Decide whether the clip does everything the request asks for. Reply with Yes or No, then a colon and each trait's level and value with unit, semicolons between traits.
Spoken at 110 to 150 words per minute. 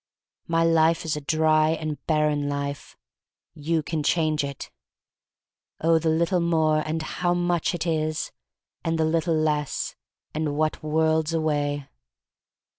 Yes: slow, 135 wpm